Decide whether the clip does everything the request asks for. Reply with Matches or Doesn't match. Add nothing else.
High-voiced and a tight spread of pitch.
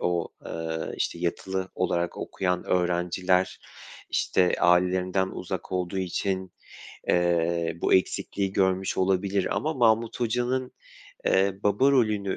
Doesn't match